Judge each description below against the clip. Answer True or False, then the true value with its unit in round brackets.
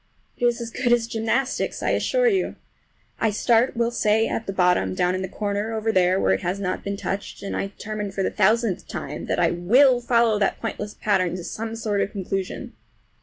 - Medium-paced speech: False (220 wpm)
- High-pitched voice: True (210 Hz)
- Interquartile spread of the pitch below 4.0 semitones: True (3.2 semitones)